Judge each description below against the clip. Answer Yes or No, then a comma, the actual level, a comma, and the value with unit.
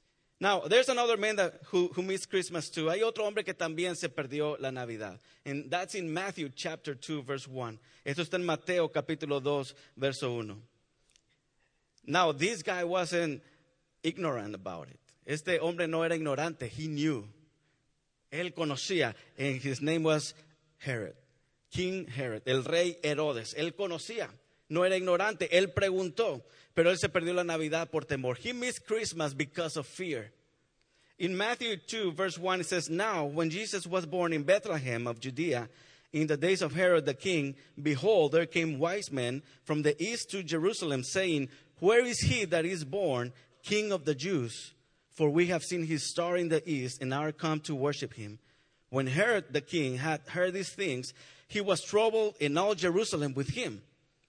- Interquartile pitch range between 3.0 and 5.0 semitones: Yes, average, 4.2 semitones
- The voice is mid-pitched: Yes, medium, 160 Hz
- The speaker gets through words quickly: No, average, 175 wpm